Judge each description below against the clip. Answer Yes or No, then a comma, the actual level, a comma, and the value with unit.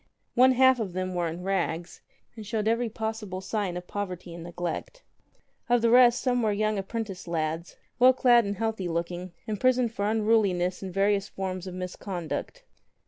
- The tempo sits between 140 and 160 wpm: No, average, 170 wpm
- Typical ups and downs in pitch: Yes, average, 4.0 semitones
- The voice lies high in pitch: Yes, high, 200 Hz